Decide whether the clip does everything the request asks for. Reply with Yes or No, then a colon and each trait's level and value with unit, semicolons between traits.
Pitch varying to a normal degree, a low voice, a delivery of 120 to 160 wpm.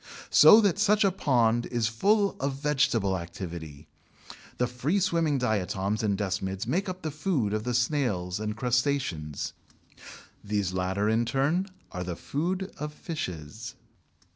No: wide, 7.6 semitones; low, 120 Hz; average, 140 wpm